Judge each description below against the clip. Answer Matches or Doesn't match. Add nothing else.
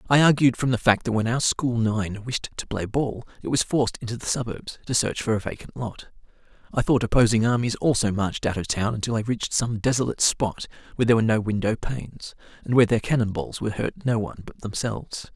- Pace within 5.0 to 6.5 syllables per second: Matches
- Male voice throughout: Matches